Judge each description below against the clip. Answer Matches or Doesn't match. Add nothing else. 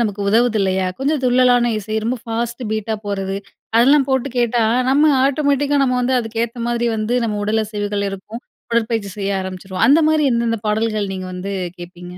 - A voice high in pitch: Matches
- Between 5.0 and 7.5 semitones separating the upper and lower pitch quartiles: Doesn't match